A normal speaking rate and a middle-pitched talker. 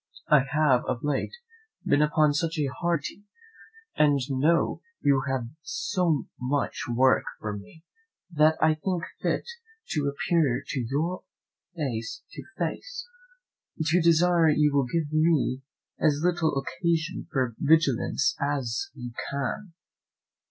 No: slow, 125 wpm; medium, 150 Hz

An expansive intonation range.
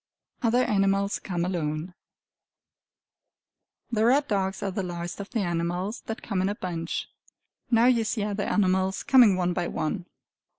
No: average, 3.5 semitones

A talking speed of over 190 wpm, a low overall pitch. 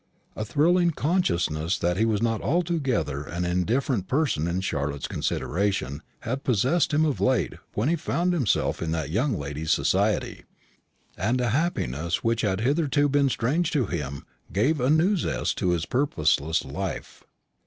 No: average, 155 wpm; low, 115 Hz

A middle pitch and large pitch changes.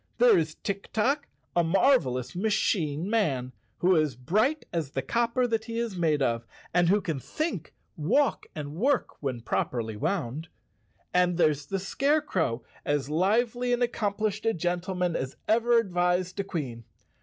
Yes: medium, 180 Hz; wide, 7.2 semitones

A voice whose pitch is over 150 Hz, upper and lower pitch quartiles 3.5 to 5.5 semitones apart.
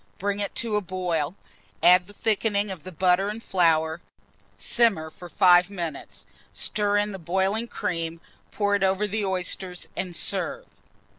No: high, 190 Hz; narrow, 2.6 semitones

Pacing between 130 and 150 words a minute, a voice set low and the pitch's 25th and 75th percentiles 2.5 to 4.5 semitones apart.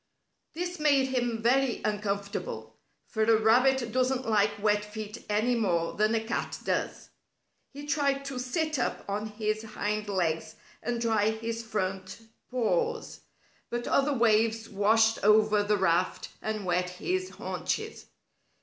No: average, 140 wpm; high, 220 Hz; average, 3.4 semitones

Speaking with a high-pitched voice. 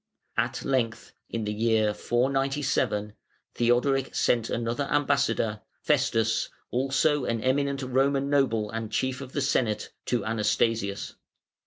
No: low, 125 Hz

